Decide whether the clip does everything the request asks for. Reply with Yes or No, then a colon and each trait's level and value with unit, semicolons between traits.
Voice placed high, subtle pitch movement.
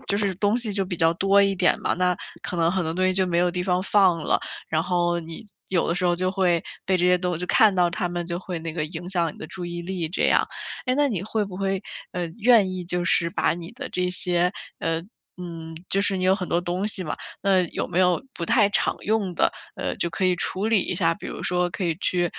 No: medium, 180 Hz; narrow, 2.0 semitones